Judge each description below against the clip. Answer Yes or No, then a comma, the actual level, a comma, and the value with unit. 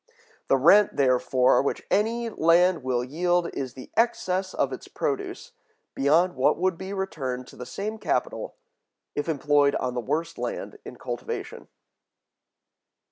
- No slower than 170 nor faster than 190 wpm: No, average, 140 wpm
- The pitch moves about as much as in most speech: No, wide, 6.6 semitones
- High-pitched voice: No, medium, 165 Hz